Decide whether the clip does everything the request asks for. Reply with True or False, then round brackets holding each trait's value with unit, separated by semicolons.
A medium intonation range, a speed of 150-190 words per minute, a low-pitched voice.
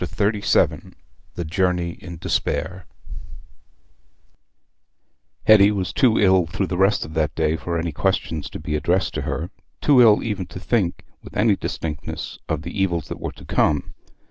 True (3.7 semitones; 160 wpm; 90 Hz)